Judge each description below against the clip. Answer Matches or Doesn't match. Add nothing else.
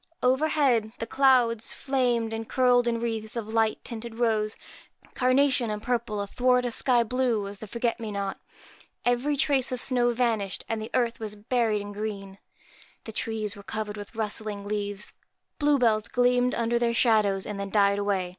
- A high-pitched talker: Matches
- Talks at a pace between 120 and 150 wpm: Doesn't match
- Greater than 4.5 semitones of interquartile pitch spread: Doesn't match